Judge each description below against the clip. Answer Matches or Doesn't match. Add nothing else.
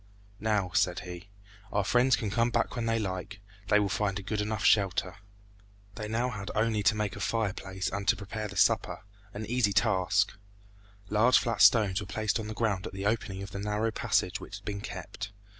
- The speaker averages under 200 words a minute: Doesn't match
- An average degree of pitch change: Doesn't match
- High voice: Doesn't match